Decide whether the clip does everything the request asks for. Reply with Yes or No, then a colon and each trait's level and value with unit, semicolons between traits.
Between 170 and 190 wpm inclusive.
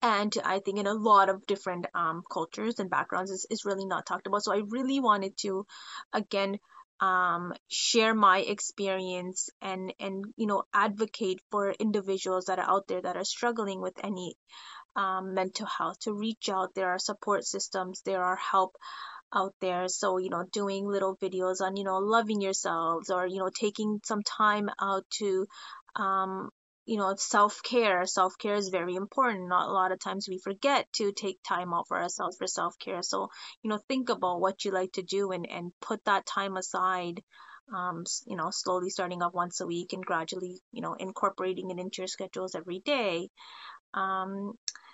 Yes: average, 185 wpm